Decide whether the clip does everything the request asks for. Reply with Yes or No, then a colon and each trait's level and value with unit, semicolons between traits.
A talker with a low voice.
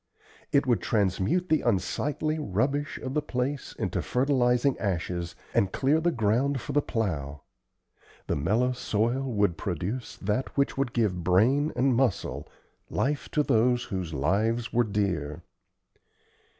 Yes: low, 120 Hz